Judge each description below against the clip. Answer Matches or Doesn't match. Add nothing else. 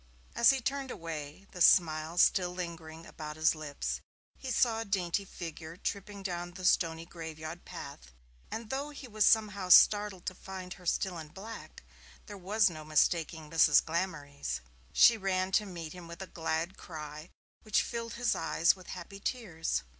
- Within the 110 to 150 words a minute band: Doesn't match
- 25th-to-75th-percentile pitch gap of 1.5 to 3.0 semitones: Doesn't match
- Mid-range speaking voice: Matches